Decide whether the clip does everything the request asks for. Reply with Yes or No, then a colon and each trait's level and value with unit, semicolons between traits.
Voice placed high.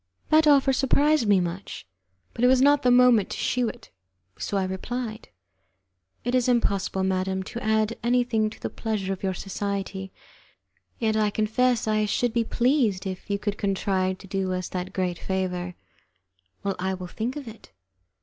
Yes: high, 210 Hz